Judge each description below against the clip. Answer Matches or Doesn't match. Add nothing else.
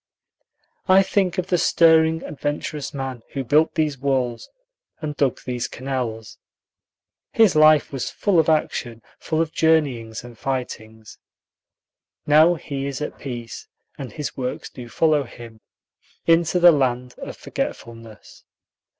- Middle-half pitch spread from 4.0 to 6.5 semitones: Matches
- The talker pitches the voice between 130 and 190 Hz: Matches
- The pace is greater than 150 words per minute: Doesn't match